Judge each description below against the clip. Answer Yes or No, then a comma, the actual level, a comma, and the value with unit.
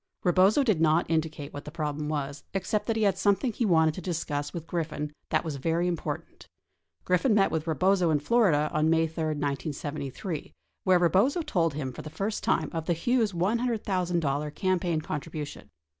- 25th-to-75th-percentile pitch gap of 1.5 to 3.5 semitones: No, average, 4.0 semitones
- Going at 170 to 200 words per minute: Yes, average, 180 wpm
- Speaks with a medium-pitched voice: Yes, medium, 165 Hz